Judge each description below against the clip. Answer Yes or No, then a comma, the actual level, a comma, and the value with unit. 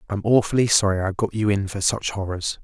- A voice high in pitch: No, low, 105 Hz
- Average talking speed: No, fast, 230 wpm